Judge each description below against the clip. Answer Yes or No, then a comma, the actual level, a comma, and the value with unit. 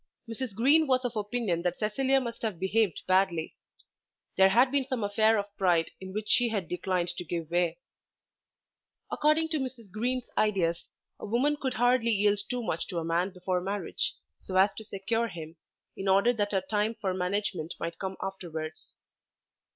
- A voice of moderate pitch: No, high, 205 Hz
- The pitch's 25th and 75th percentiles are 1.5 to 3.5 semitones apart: No, average, 4.6 semitones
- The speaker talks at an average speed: Yes, average, 175 wpm